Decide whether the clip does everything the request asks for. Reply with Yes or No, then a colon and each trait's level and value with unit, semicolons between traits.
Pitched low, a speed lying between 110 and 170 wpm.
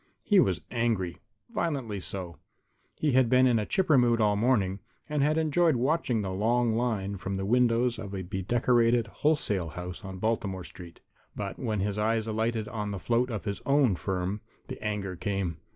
No: low, 110 Hz; average, 180 wpm